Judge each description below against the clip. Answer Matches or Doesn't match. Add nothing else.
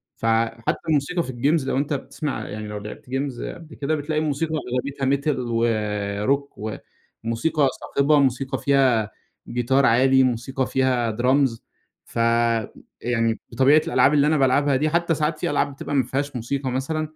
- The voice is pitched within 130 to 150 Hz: Matches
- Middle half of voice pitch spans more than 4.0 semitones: Doesn't match